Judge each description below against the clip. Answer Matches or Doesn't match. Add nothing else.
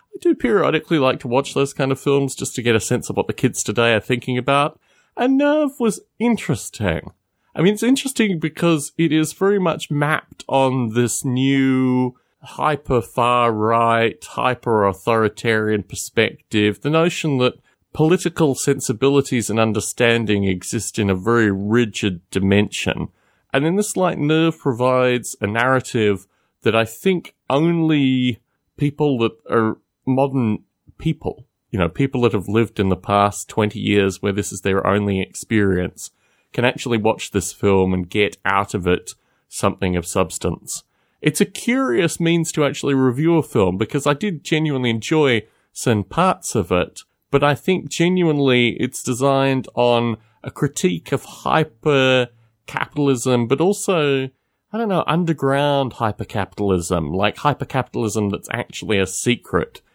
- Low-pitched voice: Matches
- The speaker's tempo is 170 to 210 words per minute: Doesn't match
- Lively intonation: Matches